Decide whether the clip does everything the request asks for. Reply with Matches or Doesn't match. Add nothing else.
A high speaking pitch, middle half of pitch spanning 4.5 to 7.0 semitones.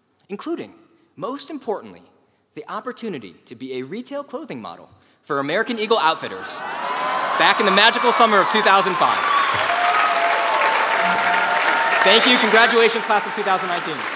Matches